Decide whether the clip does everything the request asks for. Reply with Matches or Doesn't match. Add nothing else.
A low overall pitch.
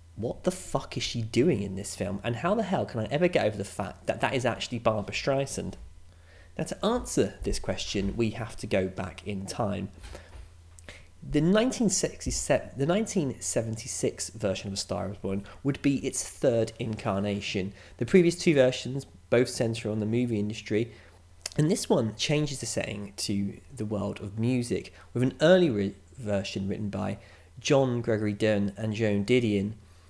Matches